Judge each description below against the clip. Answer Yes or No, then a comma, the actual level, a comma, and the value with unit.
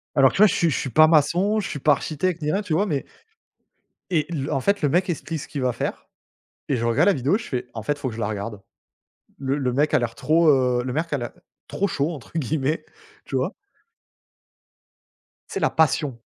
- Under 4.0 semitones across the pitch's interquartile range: No, average, 4.4 semitones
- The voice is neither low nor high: Yes, medium, 145 Hz